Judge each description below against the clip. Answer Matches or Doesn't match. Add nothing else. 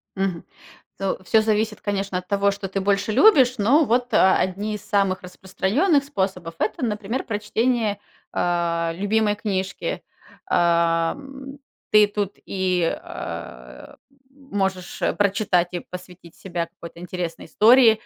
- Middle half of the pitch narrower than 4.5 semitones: Matches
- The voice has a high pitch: Matches